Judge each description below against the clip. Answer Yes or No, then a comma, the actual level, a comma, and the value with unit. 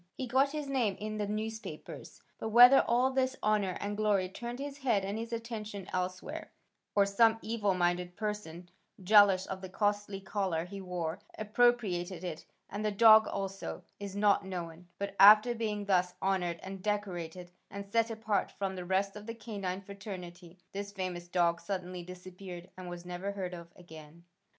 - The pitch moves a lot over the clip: No, average, 3.0 semitones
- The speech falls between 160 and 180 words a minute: Yes, average, 170 wpm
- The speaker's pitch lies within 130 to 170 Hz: No, high, 200 Hz